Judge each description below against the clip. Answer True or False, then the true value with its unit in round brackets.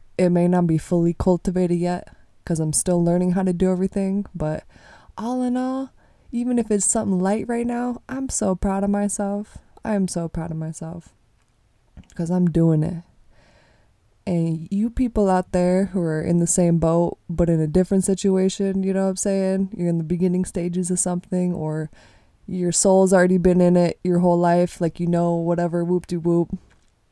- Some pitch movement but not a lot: False (2.3 semitones)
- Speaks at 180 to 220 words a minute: True (190 wpm)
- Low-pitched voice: False (180 Hz)